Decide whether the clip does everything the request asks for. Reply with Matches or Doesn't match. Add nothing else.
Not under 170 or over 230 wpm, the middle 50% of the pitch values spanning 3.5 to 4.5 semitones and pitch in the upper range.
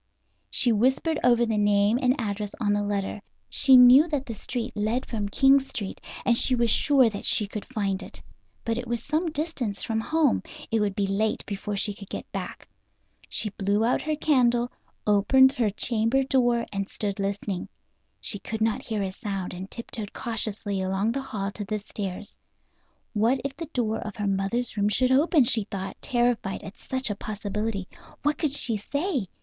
Matches